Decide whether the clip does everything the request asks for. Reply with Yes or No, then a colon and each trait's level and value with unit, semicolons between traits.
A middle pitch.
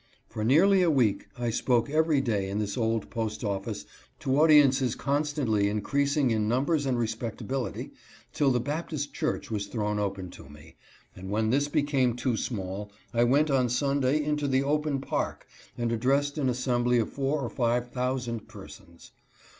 No: low, 125 Hz